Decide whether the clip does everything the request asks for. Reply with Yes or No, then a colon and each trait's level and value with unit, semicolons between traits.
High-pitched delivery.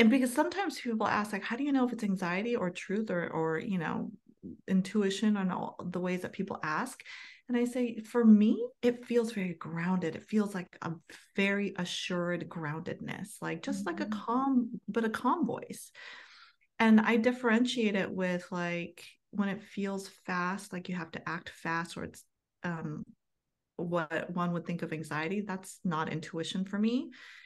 Yes: high, 200 Hz